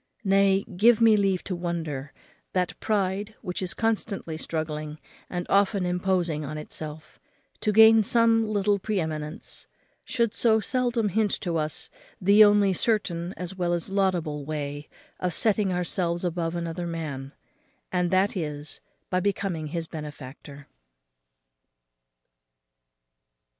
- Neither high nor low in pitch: Yes, medium, 180 Hz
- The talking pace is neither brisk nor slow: No, slow, 125 wpm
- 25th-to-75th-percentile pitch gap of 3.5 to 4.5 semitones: Yes, average, 4.2 semitones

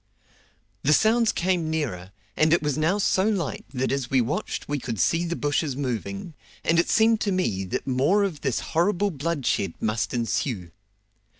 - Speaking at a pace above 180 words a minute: No, average, 175 wpm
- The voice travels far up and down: Yes, wide, 6.1 semitones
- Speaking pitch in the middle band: Yes, medium, 150 Hz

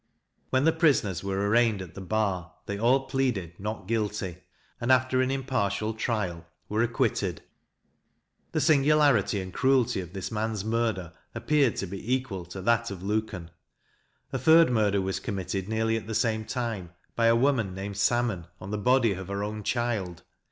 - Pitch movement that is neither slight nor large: Yes, average, 3.9 semitones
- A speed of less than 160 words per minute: No, average, 170 wpm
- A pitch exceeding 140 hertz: No, low, 110 Hz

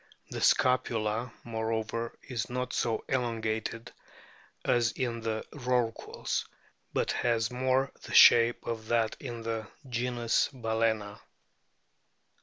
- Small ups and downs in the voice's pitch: Yes, narrow, 1.8 semitones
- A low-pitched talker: Yes, low, 115 Hz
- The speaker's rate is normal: No, slow, 105 wpm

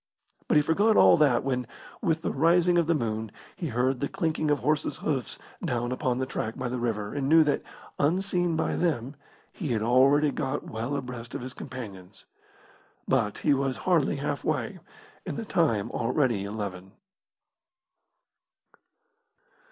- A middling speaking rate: Yes, average, 155 wpm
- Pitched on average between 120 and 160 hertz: Yes, low, 135 Hz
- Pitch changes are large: No, average, 4.6 semitones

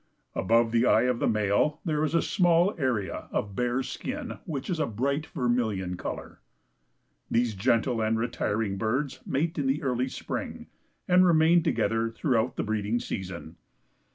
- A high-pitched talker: No, low, 125 Hz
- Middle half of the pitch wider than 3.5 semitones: Yes, average, 5.3 semitones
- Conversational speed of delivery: Yes, average, 155 wpm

